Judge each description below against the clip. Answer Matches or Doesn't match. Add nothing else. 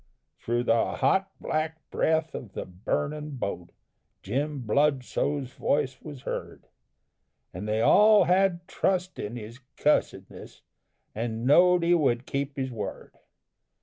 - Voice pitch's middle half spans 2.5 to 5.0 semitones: Doesn't match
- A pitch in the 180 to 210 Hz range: Doesn't match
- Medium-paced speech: Doesn't match